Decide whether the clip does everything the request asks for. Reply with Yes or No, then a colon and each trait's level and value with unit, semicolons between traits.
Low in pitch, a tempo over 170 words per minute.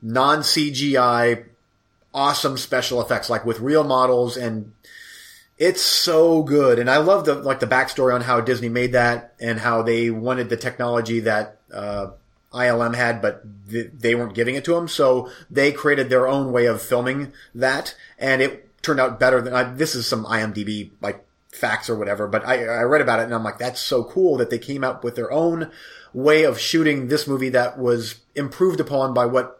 Yes: low, 125 Hz; average, 195 wpm